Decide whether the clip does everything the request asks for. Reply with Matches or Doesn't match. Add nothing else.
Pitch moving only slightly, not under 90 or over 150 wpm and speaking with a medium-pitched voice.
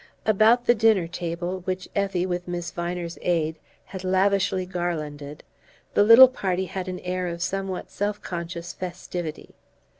Matches